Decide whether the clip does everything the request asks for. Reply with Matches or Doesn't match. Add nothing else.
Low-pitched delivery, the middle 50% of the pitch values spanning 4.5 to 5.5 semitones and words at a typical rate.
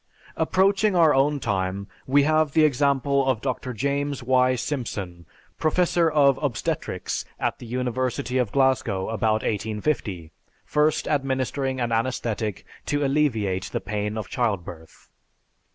Doesn't match